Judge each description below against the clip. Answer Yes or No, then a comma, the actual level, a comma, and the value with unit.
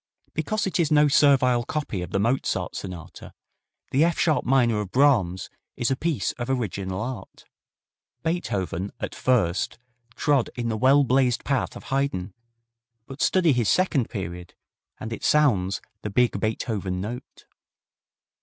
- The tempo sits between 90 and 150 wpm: Yes, average, 145 wpm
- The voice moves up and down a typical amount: No, wide, 6.1 semitones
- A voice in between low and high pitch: No, low, 125 Hz